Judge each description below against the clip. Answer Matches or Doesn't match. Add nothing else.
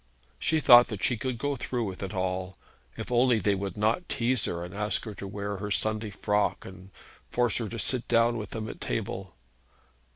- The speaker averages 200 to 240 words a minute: Matches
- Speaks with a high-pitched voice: Doesn't match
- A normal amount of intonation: Matches